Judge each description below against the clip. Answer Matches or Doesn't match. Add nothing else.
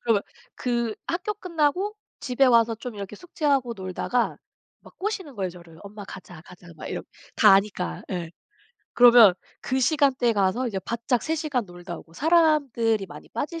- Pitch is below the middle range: Doesn't match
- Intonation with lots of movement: Matches